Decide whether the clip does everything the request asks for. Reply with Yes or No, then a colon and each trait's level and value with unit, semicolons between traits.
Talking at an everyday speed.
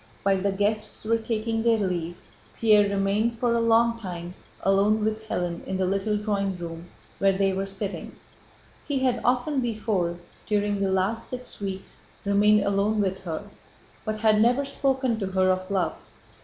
Yes: average, 170 wpm